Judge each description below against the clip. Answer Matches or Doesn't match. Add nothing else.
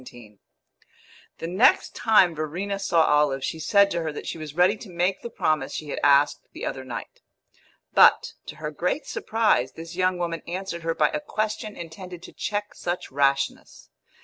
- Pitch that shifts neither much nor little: Matches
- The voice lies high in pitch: Doesn't match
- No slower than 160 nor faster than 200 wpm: Matches